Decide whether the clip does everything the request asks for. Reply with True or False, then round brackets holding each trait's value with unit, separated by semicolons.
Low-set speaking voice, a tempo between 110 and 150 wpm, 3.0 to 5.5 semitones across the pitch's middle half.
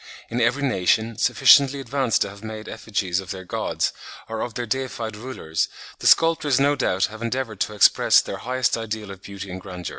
False (110 Hz; 190 wpm; 4.4 semitones)